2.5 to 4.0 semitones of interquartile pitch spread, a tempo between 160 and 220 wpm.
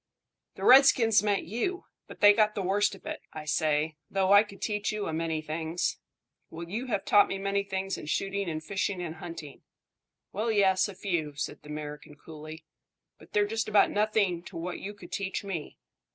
No: average, 4.4 semitones; average, 195 wpm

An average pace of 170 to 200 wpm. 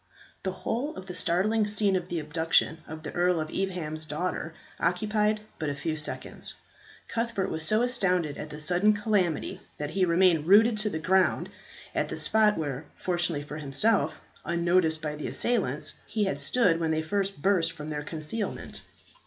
Yes: average, 175 wpm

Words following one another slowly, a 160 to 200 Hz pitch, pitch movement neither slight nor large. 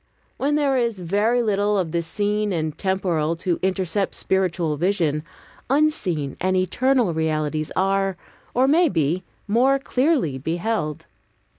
No: slow, 130 wpm; high, 190 Hz; wide, 6.1 semitones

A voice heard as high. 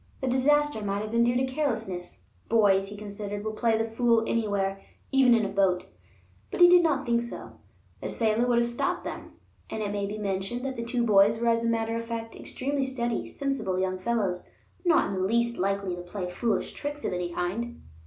Yes: high, 225 Hz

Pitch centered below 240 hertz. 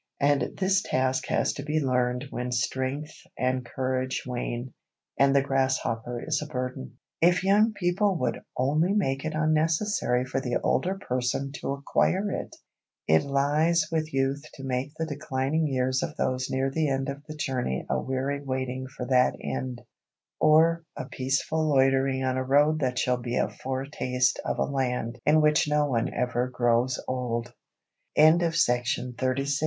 Yes: low, 135 Hz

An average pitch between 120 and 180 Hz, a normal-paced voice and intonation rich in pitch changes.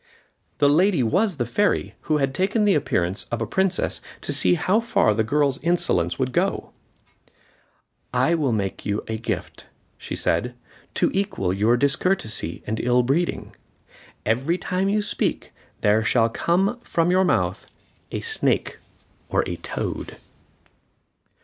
Yes: medium, 140 Hz; average, 145 wpm; wide, 8.7 semitones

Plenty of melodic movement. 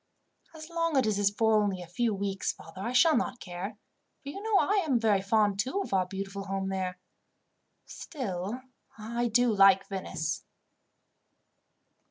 No: average, 4.3 semitones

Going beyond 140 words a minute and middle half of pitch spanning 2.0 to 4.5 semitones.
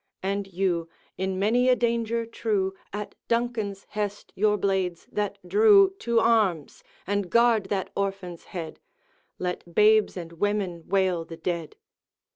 No: slow, 135 wpm; average, 3.6 semitones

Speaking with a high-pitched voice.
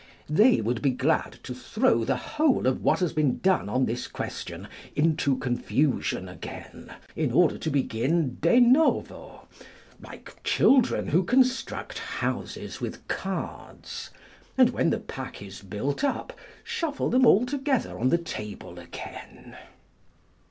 No: medium, 155 Hz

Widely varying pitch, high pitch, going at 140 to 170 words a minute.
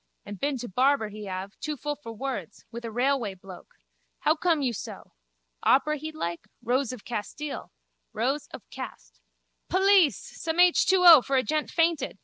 Yes: wide, 6.1 semitones; very high, 270 Hz; average, 165 wpm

